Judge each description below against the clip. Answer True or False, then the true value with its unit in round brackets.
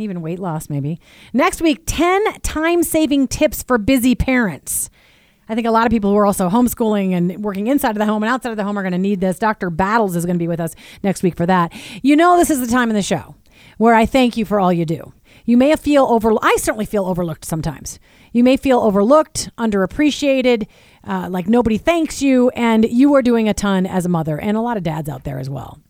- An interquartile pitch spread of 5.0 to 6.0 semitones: True (5.6 semitones)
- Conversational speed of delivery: False (245 wpm)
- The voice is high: True (220 Hz)